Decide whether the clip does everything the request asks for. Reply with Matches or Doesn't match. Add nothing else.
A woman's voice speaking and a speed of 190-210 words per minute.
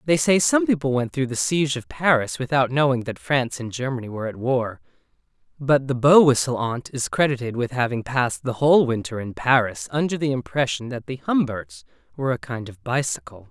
Doesn't match